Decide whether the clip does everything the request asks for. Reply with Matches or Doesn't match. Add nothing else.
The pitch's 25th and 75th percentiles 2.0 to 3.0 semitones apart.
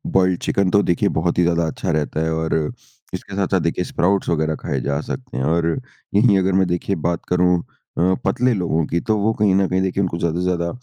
Matches